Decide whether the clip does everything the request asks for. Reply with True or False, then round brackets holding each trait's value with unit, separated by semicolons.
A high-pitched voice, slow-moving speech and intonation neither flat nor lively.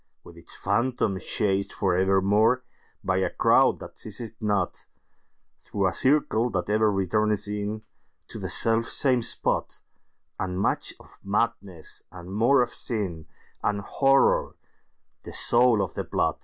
False (105 Hz; 130 wpm; 3.4 semitones)